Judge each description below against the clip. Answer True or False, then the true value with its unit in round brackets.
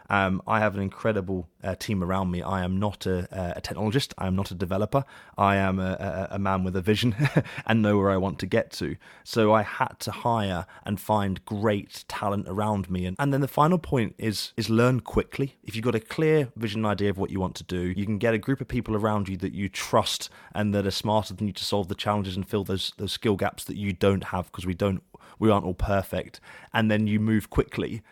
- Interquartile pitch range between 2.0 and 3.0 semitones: True (2.5 semitones)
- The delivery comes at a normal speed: False (245 wpm)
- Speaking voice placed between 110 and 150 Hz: False (100 Hz)